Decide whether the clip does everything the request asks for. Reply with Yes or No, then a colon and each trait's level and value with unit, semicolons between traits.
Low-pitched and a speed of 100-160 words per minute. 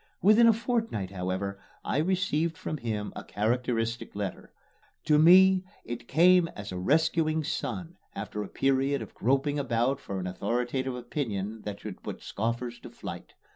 Yes: low, 125 Hz; average, 155 wpm